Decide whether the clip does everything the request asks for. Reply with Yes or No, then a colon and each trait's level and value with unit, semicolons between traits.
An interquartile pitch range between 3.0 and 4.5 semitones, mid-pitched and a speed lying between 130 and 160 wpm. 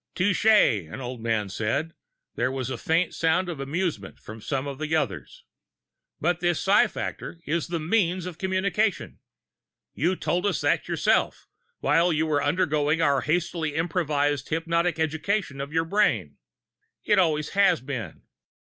Yes: average, 4.2 semitones; medium, 160 Hz; average, 155 wpm